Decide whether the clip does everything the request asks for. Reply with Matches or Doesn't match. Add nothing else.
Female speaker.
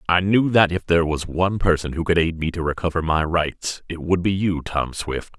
Doesn't match